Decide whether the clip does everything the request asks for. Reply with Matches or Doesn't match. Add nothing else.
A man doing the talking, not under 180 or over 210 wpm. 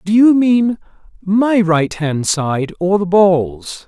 Doesn't match